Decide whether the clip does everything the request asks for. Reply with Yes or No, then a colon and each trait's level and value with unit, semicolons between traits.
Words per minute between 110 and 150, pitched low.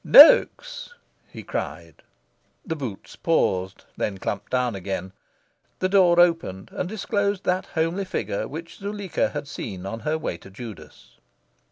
No: average, 140 wpm; medium, 160 Hz